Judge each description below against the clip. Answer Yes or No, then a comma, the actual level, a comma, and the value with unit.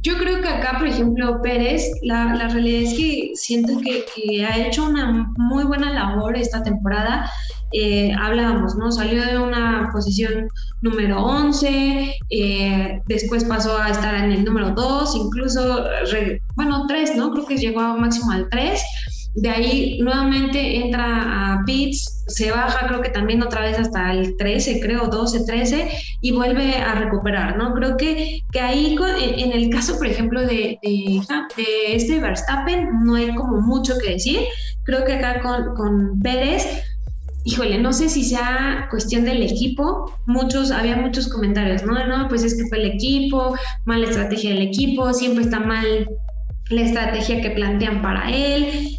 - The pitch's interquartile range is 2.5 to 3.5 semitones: Yes, average, 3.0 semitones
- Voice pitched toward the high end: Yes, high, 235 Hz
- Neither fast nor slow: Yes, average, 170 wpm